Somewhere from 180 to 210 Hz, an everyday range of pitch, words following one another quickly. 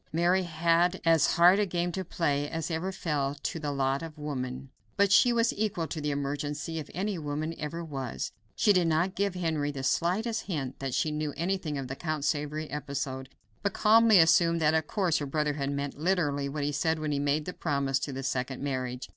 No: medium, 155 Hz; average, 3.5 semitones; fast, 220 wpm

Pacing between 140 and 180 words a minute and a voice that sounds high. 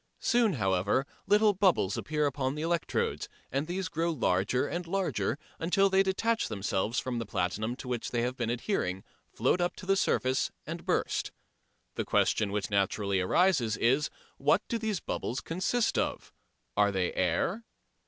No: average, 165 wpm; medium, 140 Hz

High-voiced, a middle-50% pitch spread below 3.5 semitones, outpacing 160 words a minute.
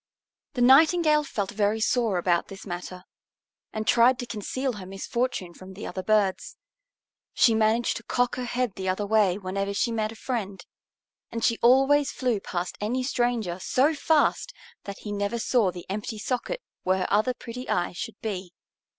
No: high, 220 Hz; average, 4.5 semitones; average, 175 wpm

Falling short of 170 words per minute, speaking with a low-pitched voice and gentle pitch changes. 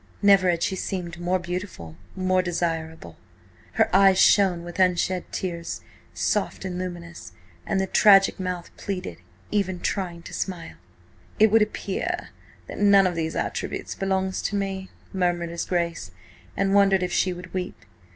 No: average, 150 wpm; medium, 185 Hz; narrow, 2.0 semitones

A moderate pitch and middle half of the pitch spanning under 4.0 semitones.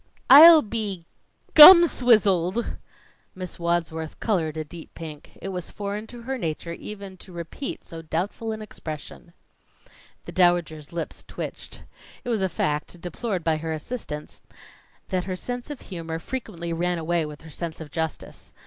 No: medium, 175 Hz; average, 4.8 semitones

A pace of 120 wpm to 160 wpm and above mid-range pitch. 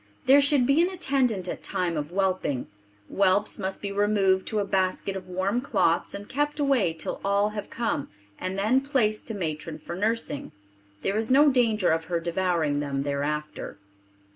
No: average, 175 wpm; high, 200 Hz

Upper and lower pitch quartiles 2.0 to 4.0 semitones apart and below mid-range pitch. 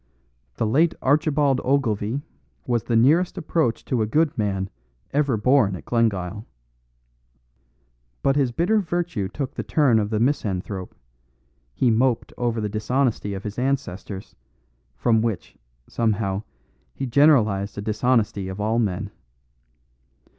No: average, 5.0 semitones; low, 115 Hz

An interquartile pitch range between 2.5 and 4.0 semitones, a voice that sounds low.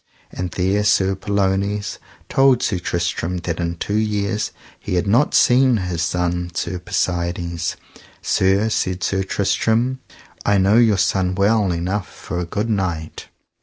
Yes: average, 2.8 semitones; very low, 95 Hz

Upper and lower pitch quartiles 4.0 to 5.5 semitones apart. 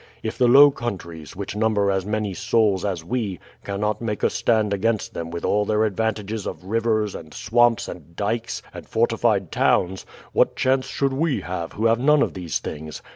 No: average, 3.4 semitones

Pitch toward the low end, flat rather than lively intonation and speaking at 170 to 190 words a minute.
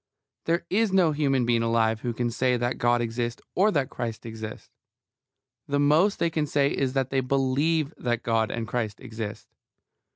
No: low, 125 Hz; average, 3.9 semitones; average, 175 wpm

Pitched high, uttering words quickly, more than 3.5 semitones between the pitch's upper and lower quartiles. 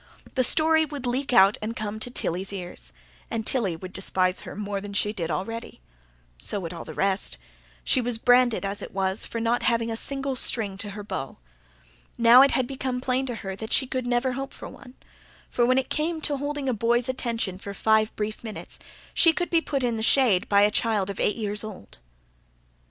Yes: high, 230 Hz; fast, 210 wpm; average, 4.2 semitones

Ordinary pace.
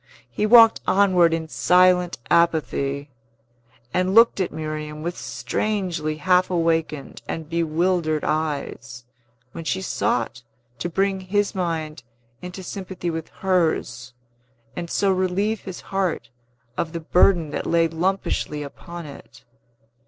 No: slow, 125 wpm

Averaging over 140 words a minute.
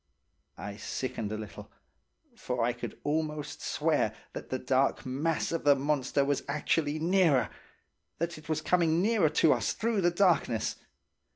Yes: average, 150 wpm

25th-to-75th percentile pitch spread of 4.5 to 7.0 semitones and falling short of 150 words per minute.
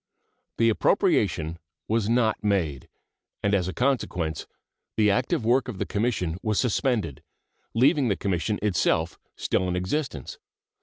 Yes: average, 5.1 semitones; slow, 135 wpm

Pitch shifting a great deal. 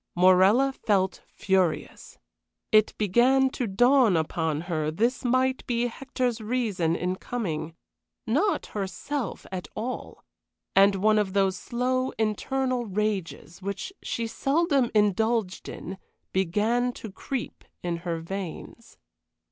No: average, 4.9 semitones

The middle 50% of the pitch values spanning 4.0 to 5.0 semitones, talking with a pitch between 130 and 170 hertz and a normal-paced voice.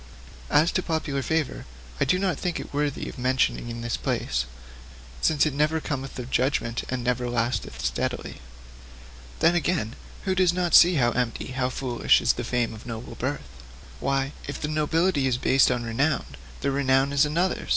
Yes: average, 4.4 semitones; low, 135 Hz; average, 180 wpm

